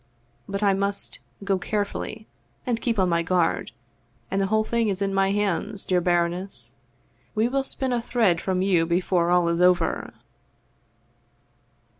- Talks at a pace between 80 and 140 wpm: No, average, 155 wpm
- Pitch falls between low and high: No, high, 195 Hz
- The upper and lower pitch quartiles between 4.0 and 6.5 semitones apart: No, average, 3.2 semitones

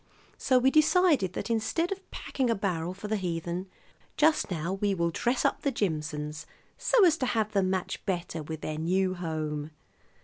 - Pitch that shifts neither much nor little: No, wide, 7.0 semitones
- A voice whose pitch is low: No, high, 190 Hz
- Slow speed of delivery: No, average, 180 wpm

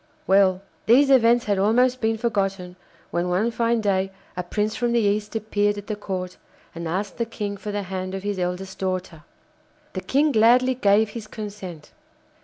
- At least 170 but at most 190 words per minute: Yes, average, 180 wpm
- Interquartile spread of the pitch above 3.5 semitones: No, average, 3.2 semitones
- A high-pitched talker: Yes, high, 205 Hz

